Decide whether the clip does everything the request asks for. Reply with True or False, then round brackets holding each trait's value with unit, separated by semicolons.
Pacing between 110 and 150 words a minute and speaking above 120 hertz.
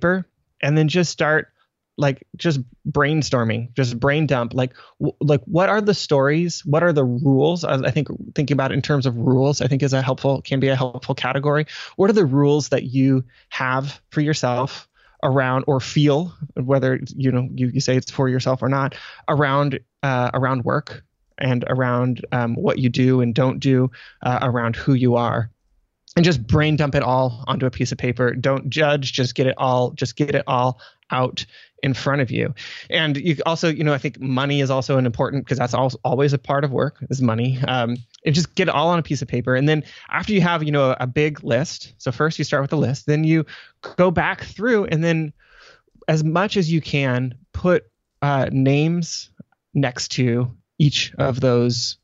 False (205 wpm; 135 Hz)